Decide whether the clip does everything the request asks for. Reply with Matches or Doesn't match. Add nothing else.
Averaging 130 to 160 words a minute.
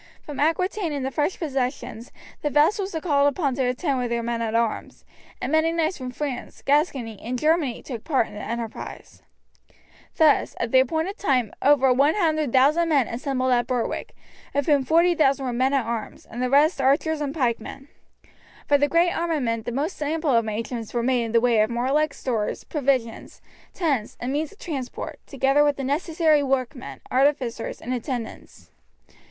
Doesn't match